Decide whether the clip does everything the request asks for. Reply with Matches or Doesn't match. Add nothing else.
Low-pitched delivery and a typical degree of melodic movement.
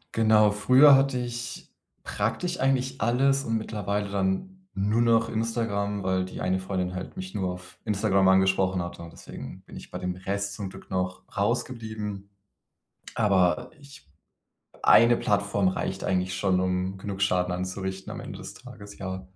Matches